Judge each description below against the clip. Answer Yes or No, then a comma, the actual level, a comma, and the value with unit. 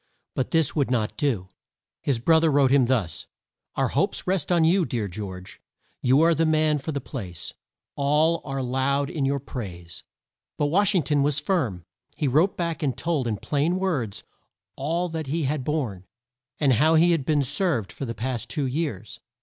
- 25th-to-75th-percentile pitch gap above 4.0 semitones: Yes, average, 4.5 semitones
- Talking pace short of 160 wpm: No, average, 190 wpm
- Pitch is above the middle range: No, medium, 140 Hz